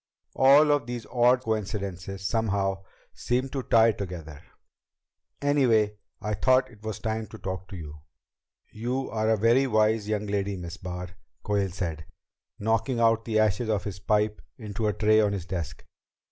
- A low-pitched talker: Yes, low, 105 Hz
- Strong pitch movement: No, average, 2.8 semitones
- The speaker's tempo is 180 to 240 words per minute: No, average, 160 wpm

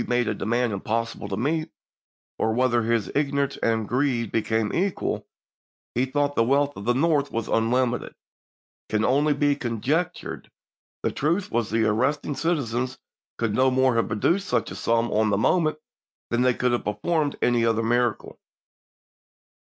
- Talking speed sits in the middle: Yes, average, 160 wpm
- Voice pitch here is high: No, low, 125 Hz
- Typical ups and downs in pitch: Yes, average, 3.9 semitones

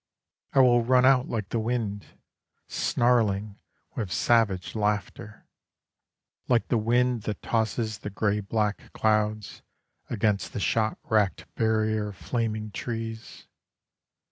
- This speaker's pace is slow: Yes, slow, 115 wpm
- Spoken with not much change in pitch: Yes, narrow, 1.9 semitones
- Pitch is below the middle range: Yes, low, 110 Hz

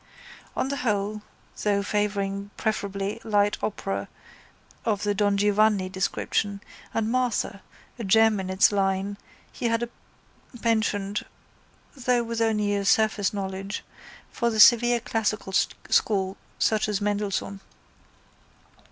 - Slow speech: Yes, slow, 120 wpm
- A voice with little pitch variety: Yes, narrow, 1.9 semitones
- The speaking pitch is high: Yes, high, 205 Hz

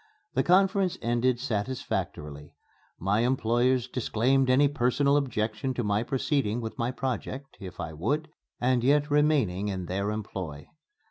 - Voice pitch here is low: Yes, low, 120 Hz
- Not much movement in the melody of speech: No, average, 4.7 semitones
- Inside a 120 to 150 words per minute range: Yes, slow, 135 wpm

